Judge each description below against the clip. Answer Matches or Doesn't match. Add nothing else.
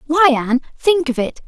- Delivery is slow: Doesn't match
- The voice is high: Matches